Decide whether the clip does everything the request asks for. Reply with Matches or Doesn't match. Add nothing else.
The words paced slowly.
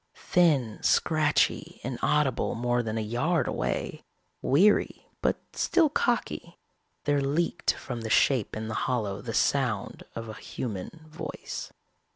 Matches